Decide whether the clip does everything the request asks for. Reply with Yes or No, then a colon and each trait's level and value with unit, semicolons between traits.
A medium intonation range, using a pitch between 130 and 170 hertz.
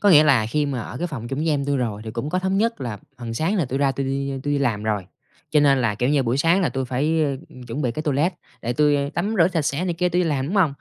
Yes: average, 4.7 semitones; medium, 140 Hz